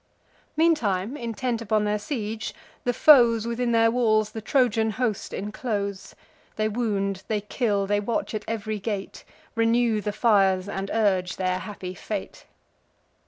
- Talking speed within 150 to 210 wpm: No, average, 140 wpm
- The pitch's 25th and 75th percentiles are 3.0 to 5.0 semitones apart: No, narrow, 2.4 semitones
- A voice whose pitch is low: No, high, 215 Hz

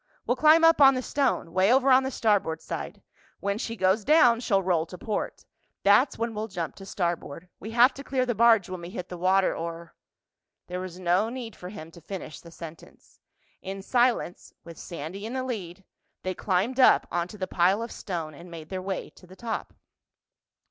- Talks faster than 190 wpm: Yes, average, 200 wpm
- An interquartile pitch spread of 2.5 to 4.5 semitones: No, average, 5.1 semitones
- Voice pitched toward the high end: Yes, high, 195 Hz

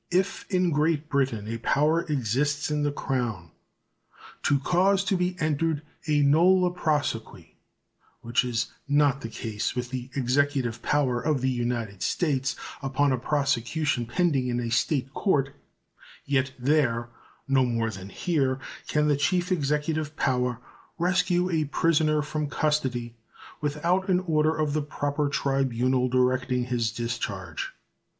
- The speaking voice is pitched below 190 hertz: Yes, medium, 140 Hz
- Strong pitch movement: No, average, 3.8 semitones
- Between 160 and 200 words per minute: No, average, 140 wpm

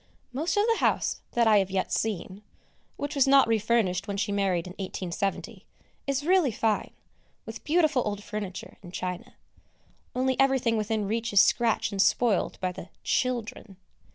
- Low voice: No, high, 220 Hz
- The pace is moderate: Yes, average, 160 wpm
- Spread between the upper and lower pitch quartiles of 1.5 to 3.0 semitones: No, average, 4.5 semitones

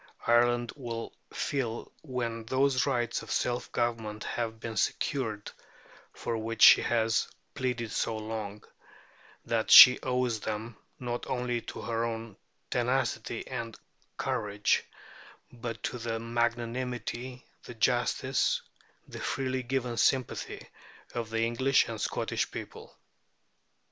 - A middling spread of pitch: No, narrow, 1.7 semitones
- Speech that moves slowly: Yes, slow, 120 wpm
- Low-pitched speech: Yes, low, 120 Hz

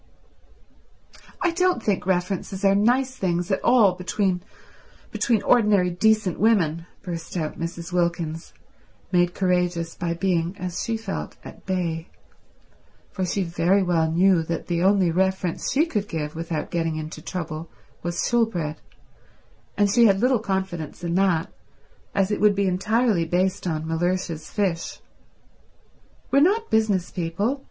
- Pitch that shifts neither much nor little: Yes, average, 3.4 semitones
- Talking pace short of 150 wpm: Yes, average, 140 wpm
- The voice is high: No, medium, 180 Hz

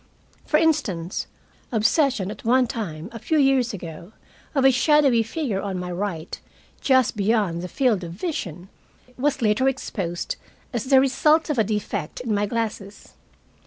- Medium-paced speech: Yes, average, 155 wpm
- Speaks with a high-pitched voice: Yes, high, 225 Hz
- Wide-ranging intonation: Yes, wide, 5.8 semitones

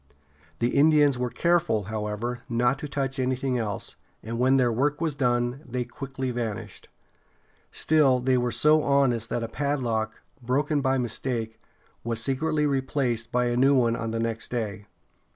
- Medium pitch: No, low, 125 Hz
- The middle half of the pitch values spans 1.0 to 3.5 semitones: Yes, average, 3.1 semitones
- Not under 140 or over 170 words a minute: Yes, average, 160 wpm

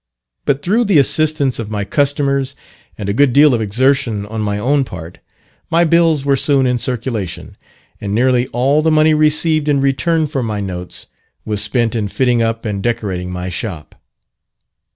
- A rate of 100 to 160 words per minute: No, average, 175 wpm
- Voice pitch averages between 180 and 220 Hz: No, low, 125 Hz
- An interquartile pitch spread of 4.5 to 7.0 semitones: Yes, wide, 5.4 semitones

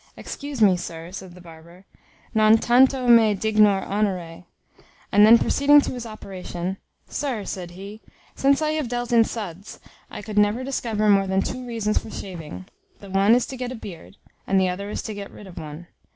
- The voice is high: Yes, high, 210 Hz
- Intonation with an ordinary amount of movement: Yes, average, 4.1 semitones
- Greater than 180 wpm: Yes, average, 190 wpm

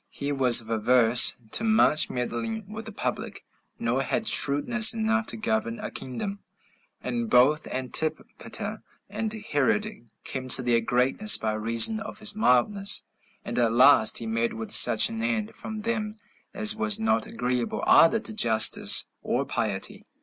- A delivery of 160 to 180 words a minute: No, average, 150 wpm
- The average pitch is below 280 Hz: Yes, high, 190 Hz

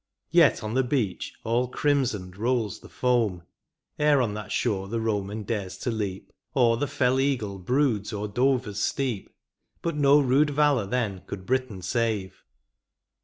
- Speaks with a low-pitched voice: Yes, low, 115 Hz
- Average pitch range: Yes, average, 4.3 semitones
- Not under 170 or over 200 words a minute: No, average, 160 wpm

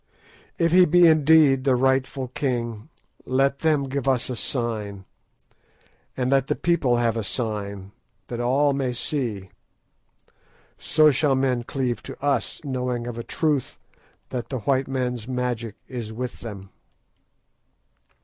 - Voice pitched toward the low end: Yes, low, 130 Hz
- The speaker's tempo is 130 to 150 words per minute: Yes, average, 140 wpm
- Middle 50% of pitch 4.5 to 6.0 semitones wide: No, average, 2.7 semitones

